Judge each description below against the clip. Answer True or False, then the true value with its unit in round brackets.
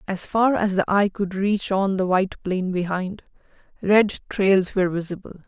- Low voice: False (190 Hz)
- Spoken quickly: False (175 wpm)